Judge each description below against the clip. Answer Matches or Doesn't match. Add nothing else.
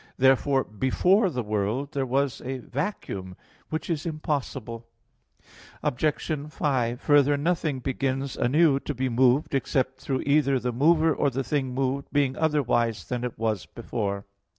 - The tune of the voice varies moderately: Matches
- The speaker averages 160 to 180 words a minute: Doesn't match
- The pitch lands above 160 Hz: Doesn't match